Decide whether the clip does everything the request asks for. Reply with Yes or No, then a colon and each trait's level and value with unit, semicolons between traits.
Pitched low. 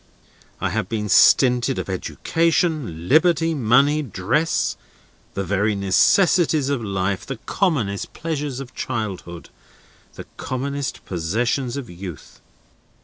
Yes: low, 125 Hz